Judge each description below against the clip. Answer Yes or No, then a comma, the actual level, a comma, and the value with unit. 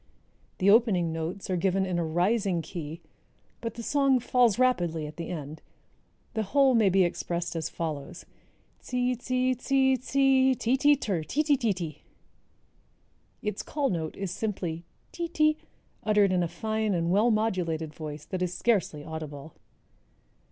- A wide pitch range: Yes, wide, 6.9 semitones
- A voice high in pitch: Yes, high, 195 Hz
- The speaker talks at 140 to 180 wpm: Yes, average, 160 wpm